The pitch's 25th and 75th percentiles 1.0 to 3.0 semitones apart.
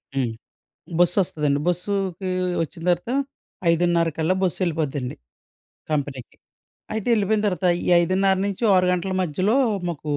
No: average, 3.7 semitones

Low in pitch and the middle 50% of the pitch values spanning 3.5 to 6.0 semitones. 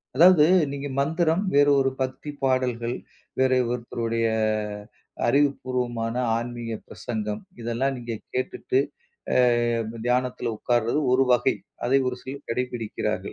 No: low, 125 Hz; narrow, 2.4 semitones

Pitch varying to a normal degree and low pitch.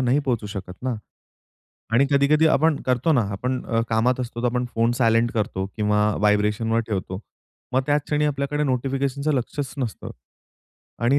Yes: average, 3.7 semitones; low, 125 Hz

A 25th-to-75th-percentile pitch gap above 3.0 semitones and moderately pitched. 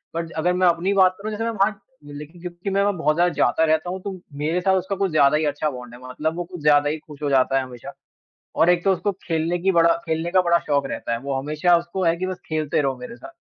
Yes: average, 3.6 semitones; medium, 170 Hz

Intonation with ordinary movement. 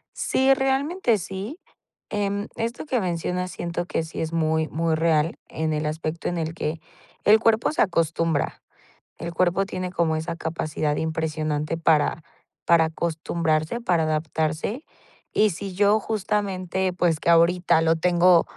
Yes: average, 3.7 semitones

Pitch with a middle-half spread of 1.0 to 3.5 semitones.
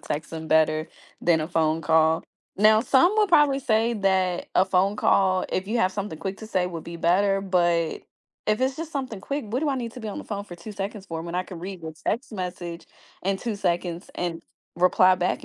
No: average, 4.2 semitones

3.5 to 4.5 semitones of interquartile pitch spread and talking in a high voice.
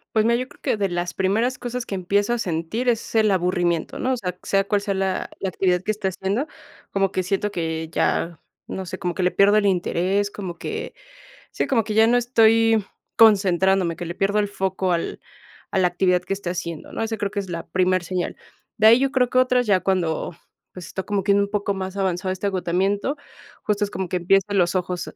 No: average, 2.8 semitones; high, 195 Hz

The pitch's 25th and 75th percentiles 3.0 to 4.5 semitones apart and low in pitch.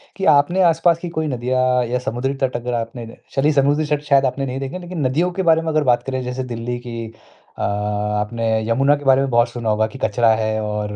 Yes: average, 4.0 semitones; low, 130 Hz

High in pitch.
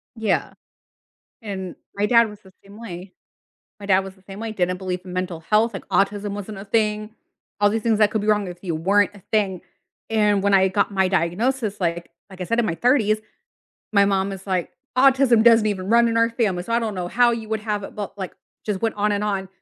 Yes: high, 205 Hz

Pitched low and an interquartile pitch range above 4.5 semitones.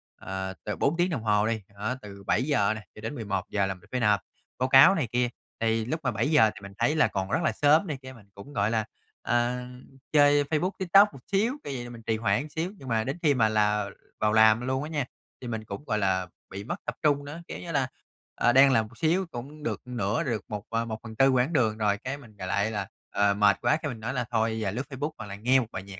Yes: low, 115 Hz; average, 5.0 semitones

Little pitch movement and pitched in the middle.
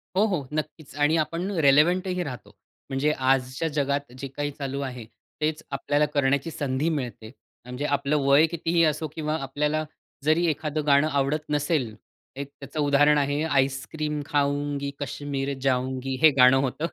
Yes: narrow, 2.0 semitones; medium, 145 Hz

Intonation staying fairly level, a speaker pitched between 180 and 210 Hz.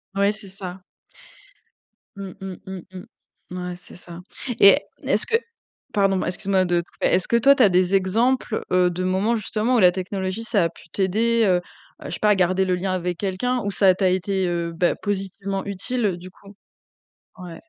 Yes: narrow, 2.1 semitones; high, 190 Hz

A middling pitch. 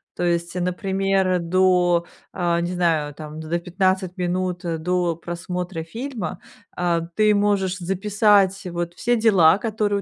Yes: medium, 180 Hz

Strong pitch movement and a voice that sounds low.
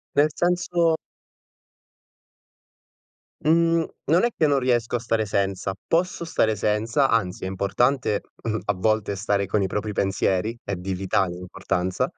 Yes: wide, 6.4 semitones; low, 110 Hz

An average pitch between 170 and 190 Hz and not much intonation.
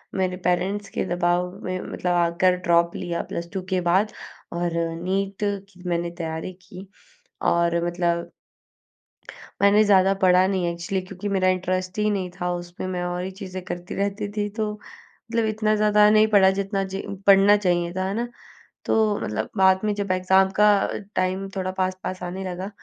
Yes: medium, 185 Hz; narrow, 2.0 semitones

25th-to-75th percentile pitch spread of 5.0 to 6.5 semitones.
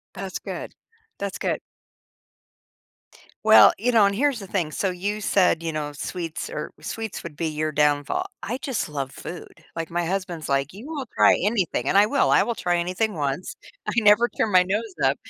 Yes: average, 5.3 semitones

